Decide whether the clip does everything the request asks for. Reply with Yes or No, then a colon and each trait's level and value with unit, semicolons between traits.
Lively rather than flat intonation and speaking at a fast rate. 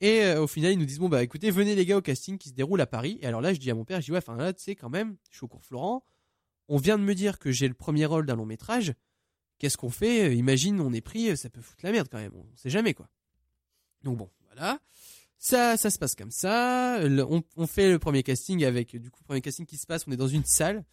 Yes: wide, 7.8 semitones; fast, 285 wpm